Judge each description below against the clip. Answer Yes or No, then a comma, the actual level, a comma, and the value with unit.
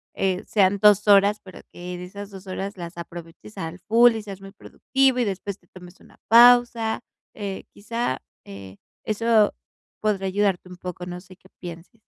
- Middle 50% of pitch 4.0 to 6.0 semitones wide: No, average, 2.9 semitones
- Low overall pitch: No, high, 195 Hz